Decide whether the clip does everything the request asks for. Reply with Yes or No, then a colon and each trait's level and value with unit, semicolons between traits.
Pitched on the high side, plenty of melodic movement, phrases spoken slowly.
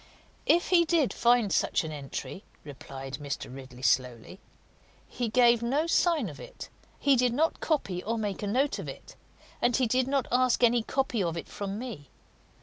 No: high, 235 Hz; wide, 7.8 semitones; average, 180 wpm